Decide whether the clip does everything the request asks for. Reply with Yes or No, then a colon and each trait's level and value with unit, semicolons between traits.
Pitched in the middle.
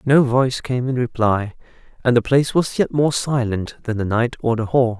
No: low, 125 Hz